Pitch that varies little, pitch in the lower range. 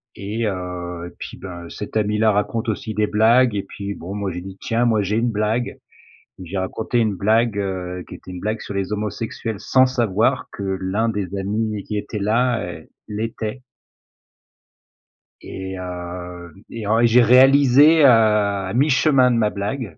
No: average, 3.3 semitones; low, 105 Hz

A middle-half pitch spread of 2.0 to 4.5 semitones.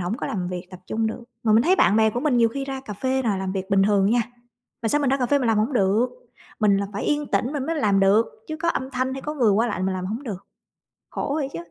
No: average, 5.1 semitones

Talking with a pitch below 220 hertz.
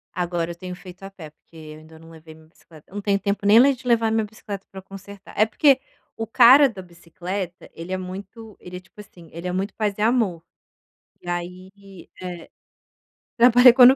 Yes: high, 190 Hz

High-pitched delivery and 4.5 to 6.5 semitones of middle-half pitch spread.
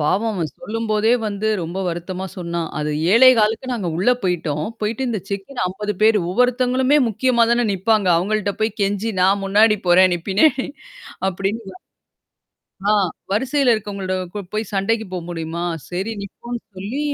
No: high, 210 Hz; average, 3.6 semitones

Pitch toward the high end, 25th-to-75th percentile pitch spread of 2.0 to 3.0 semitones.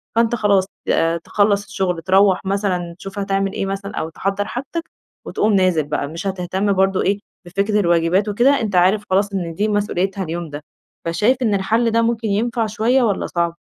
Yes: high, 195 Hz; average, 2.7 semitones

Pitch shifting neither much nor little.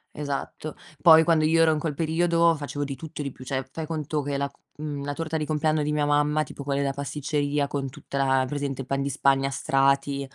No: narrow, 2.0 semitones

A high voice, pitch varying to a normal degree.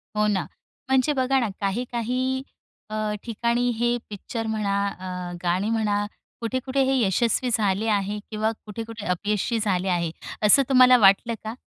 Yes: high, 220 Hz; average, 3.3 semitones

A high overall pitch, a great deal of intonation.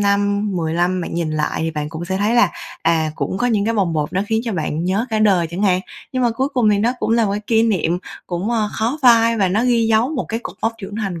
No: high, 205 Hz; average, 4.7 semitones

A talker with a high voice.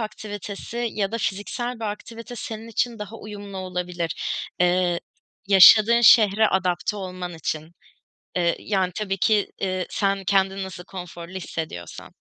Yes: high, 195 Hz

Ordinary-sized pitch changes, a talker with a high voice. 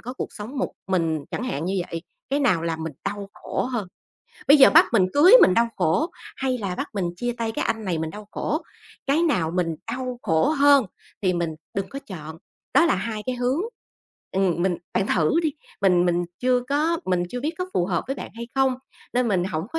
No: wide, 7.1 semitones; high, 210 Hz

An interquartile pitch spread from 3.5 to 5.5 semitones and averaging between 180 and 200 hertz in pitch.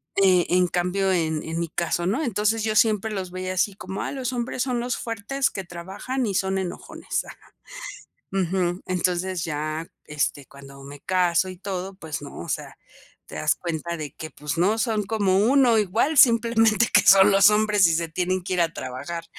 Yes: average, 4.0 semitones; medium, 185 Hz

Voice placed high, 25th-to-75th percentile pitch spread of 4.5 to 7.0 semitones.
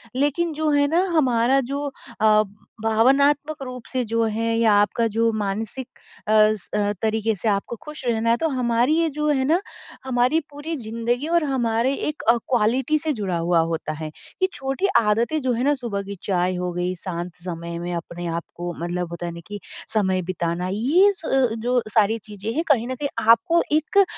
Yes: high, 230 Hz; wide, 5.5 semitones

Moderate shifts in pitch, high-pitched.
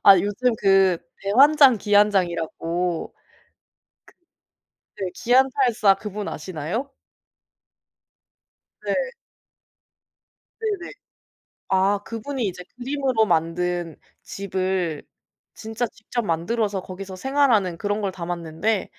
Yes: average, 4.9 semitones; high, 200 Hz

